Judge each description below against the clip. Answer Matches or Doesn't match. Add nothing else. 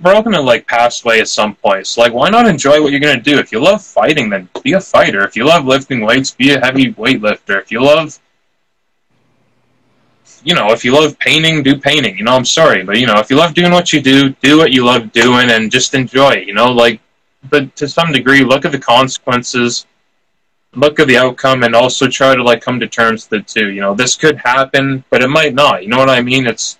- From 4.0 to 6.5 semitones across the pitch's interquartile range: Doesn't match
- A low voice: Matches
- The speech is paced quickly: Matches